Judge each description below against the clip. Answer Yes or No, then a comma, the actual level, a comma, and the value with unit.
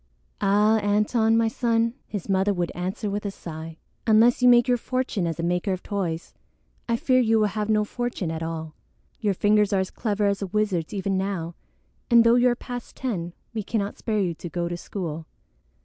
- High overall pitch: Yes, high, 205 Hz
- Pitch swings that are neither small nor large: Yes, average, 4.1 semitones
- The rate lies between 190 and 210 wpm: Yes, fast, 205 wpm